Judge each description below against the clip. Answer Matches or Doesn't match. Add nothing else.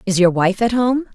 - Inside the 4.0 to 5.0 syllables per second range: Doesn't match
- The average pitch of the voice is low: Doesn't match